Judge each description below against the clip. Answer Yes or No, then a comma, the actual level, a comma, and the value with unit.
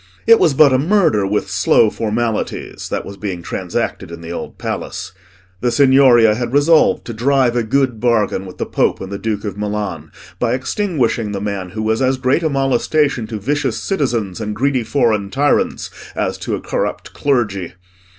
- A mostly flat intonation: No, average, 4.6 semitones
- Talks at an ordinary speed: Yes, average, 180 wpm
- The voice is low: Yes, low, 115 Hz